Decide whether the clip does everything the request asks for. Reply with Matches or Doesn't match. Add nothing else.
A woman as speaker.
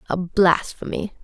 Matches